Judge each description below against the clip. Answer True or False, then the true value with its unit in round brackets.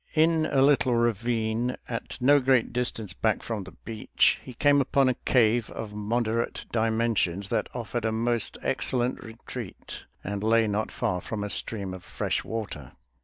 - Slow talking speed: False (165 wpm)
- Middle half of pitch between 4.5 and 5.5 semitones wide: False (2.5 semitones)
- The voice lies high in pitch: False (115 Hz)